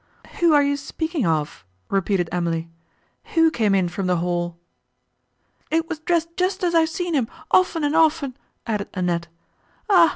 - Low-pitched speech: No, very high, 285 Hz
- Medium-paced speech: Yes, average, 165 wpm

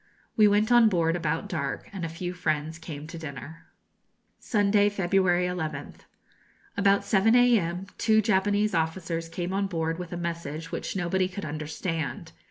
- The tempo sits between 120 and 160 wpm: Yes, average, 155 wpm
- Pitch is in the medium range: Yes, medium, 175 Hz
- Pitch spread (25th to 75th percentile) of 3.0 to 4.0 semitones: Yes, average, 3.5 semitones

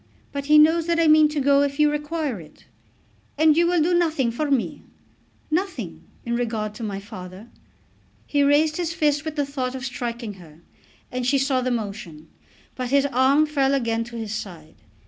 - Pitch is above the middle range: Yes, very high, 270 Hz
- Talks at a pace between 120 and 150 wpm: No, average, 190 wpm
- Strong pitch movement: No, average, 4.9 semitones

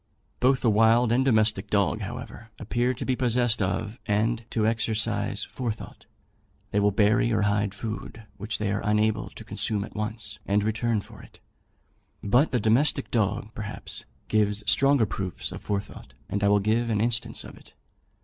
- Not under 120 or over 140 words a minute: No, average, 170 wpm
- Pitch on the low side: Yes, low, 110 Hz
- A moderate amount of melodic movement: No, narrow, 2.2 semitones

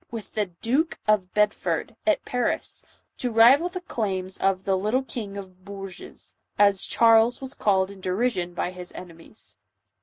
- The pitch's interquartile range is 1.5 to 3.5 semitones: No, average, 4.0 semitones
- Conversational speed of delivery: Yes, average, 170 wpm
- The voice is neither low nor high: No, high, 205 Hz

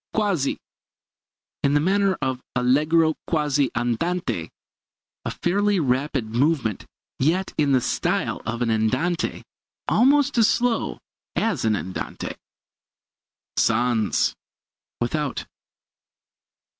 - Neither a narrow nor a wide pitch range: No, wide, 6.7 semitones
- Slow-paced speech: Yes, slow, 100 wpm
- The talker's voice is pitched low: No, medium, 145 Hz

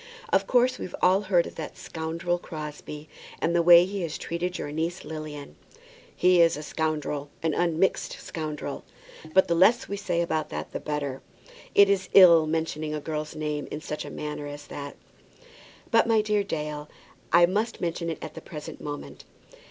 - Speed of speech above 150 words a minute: Yes, average, 180 wpm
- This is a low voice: No, medium, 160 Hz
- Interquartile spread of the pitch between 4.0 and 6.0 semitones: No, average, 2.9 semitones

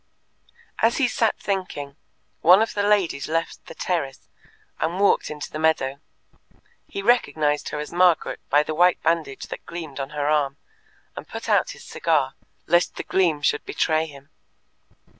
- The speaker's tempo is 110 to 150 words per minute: No, average, 160 wpm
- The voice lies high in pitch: No, medium, 160 Hz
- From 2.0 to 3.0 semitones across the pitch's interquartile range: No, average, 3.7 semitones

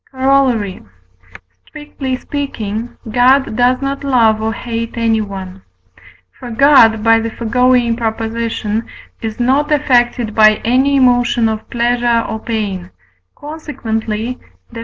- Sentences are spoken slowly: Yes, slow, 115 wpm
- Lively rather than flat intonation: No, narrow, 2.6 semitones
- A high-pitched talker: Yes, high, 235 Hz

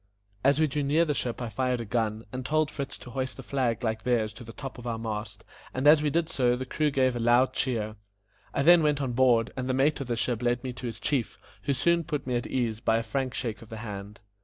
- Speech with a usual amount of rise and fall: Yes, average, 3.2 semitones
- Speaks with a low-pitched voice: Yes, low, 125 Hz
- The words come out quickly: Yes, fast, 275 wpm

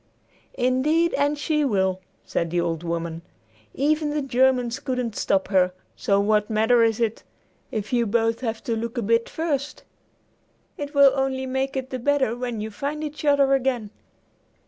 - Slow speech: No, average, 170 wpm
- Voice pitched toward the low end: No, high, 245 Hz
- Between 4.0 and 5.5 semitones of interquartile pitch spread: Yes, average, 4.3 semitones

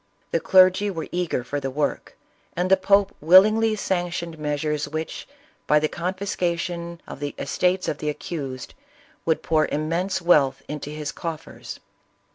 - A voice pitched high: No, medium, 170 Hz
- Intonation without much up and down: No, average, 3.5 semitones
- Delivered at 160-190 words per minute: No, average, 145 wpm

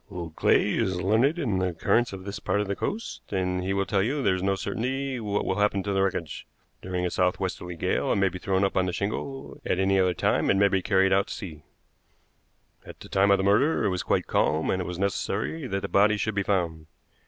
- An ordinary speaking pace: No, fast, 245 wpm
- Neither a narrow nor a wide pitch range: No, narrow, 2.0 semitones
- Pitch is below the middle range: Yes, very low, 95 Hz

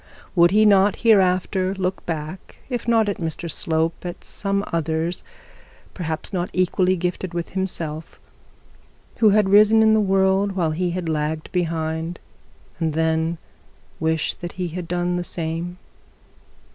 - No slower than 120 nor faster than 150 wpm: Yes, average, 145 wpm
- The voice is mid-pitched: Yes, medium, 175 Hz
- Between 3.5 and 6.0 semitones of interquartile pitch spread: No, average, 2.9 semitones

